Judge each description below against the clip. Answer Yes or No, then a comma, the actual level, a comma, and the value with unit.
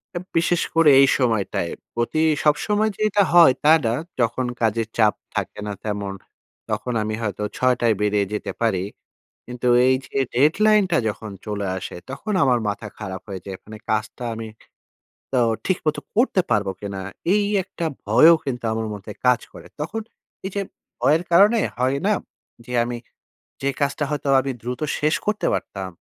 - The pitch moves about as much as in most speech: No, wide, 6.8 semitones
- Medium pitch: No, low, 125 Hz